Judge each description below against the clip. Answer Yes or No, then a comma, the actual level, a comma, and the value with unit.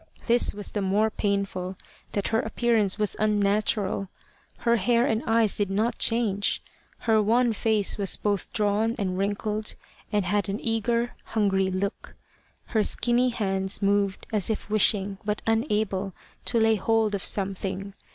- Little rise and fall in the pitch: Yes, narrow, 2.2 semitones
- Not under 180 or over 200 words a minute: No, average, 150 wpm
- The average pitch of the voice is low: No, high, 210 Hz